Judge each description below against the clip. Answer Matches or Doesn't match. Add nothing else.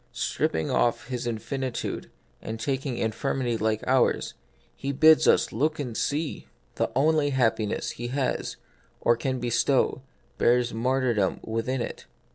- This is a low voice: Matches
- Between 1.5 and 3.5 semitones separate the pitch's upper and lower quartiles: Matches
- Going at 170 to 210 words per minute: Doesn't match